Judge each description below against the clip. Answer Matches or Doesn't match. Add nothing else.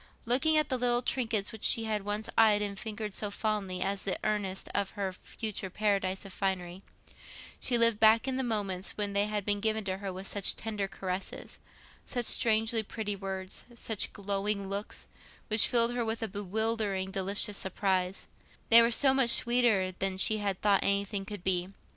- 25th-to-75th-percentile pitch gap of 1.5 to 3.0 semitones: Matches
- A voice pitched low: Doesn't match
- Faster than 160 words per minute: Matches